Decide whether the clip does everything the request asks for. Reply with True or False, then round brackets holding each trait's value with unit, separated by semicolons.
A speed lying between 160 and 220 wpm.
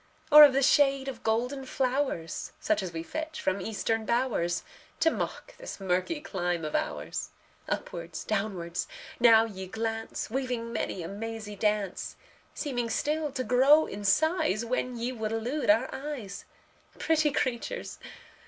False (145 wpm)